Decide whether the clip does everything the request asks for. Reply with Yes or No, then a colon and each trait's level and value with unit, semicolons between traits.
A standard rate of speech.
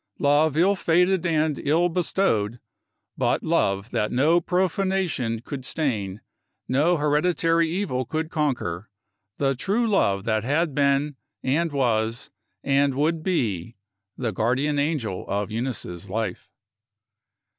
No: slow, 125 wpm